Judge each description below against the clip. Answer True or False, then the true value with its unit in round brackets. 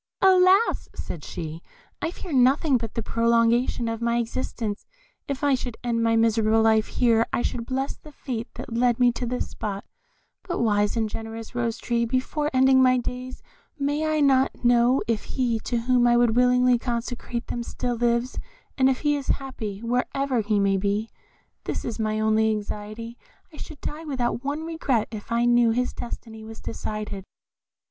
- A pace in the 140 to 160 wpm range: False (180 wpm)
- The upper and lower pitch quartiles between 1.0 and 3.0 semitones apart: True (2.5 semitones)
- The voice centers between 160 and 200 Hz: False (240 Hz)